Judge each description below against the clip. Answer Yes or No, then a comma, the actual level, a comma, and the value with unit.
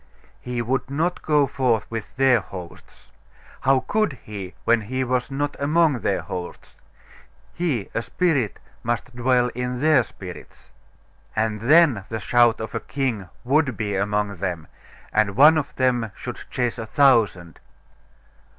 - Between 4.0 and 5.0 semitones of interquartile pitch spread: Yes, average, 4.3 semitones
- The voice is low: Yes, low, 120 Hz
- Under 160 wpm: Yes, average, 145 wpm